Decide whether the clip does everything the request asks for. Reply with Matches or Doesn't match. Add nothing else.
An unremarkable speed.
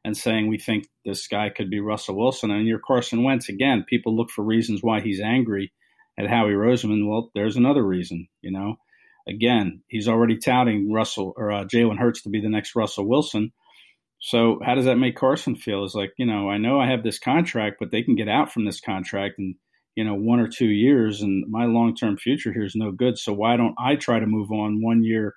Doesn't match